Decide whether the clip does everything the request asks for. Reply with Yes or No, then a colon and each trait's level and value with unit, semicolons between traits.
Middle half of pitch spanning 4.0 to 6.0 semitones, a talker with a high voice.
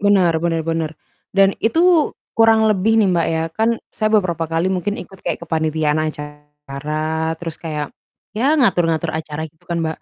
No: average, 4.4 semitones; medium, 165 Hz